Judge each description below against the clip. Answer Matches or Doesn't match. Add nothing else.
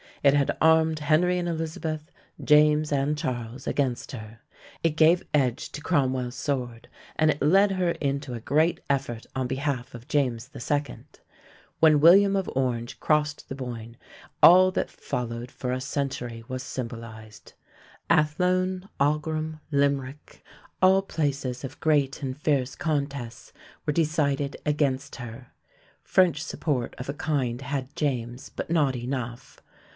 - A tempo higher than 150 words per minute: Doesn't match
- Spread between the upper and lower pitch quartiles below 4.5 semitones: Matches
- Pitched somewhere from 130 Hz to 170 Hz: Matches